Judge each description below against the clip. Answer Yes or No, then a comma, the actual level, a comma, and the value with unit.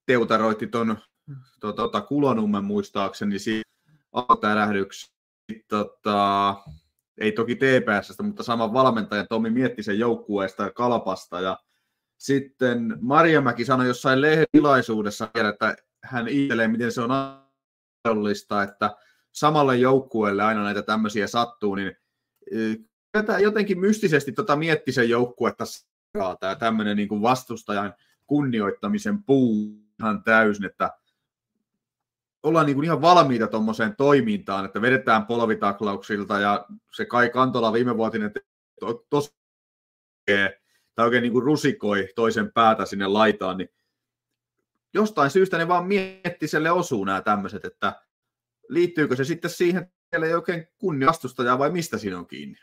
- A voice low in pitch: Yes, low, 115 Hz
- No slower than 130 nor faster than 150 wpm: No, average, 120 wpm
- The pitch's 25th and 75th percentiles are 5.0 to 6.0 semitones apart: Yes, average, 5.3 semitones